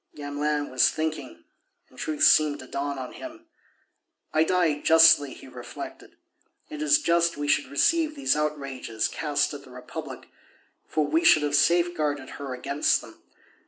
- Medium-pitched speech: Yes, medium, 150 Hz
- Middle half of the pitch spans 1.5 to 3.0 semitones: Yes, narrow, 2.4 semitones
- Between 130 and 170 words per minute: Yes, average, 155 wpm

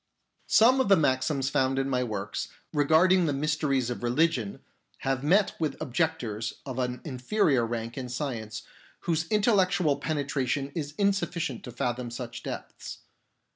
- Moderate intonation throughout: Yes, average, 4.7 semitones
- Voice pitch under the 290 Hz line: Yes, medium, 140 Hz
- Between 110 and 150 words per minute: Yes, average, 145 wpm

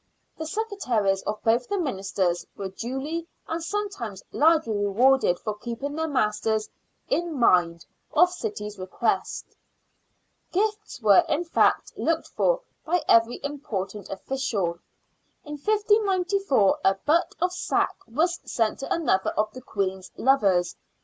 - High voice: Yes, very high, 265 Hz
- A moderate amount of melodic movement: No, wide, 8.7 semitones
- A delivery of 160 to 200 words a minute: No, slow, 135 wpm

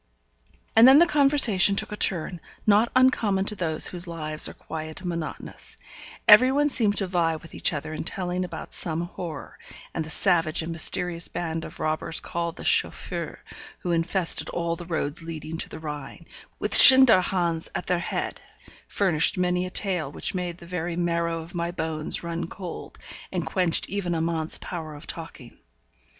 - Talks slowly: No, average, 175 wpm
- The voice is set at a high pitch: No, medium, 170 Hz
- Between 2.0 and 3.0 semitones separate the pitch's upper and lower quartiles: Yes, narrow, 2.5 semitones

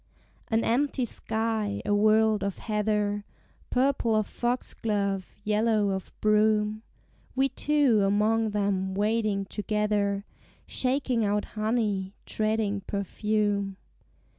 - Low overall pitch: No, high, 215 Hz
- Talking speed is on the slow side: Yes, slow, 100 wpm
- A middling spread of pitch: No, narrow, 1.7 semitones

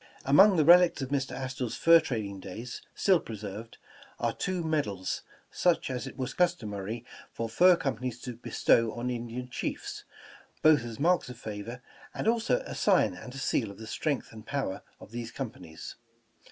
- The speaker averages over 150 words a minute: Yes, average, 180 wpm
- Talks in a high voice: No, low, 125 Hz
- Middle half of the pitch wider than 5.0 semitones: Yes, wide, 5.6 semitones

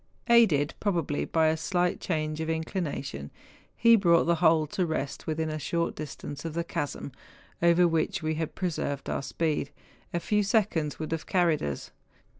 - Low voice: No, medium, 160 Hz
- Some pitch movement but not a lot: No, narrow, 2.2 semitones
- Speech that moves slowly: No, average, 175 wpm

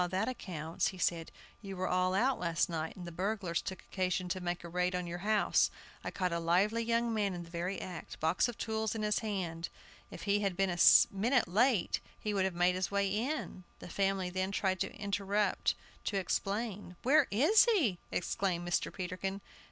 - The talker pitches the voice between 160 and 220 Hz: Yes, high, 190 Hz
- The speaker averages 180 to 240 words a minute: Yes, average, 200 wpm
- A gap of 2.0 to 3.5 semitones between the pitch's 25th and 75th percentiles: Yes, average, 2.9 semitones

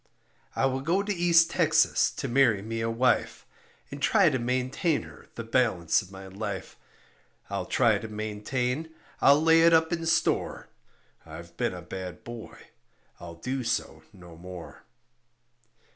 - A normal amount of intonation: No, wide, 7.1 semitones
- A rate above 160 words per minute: No, average, 155 wpm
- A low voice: Yes, low, 120 Hz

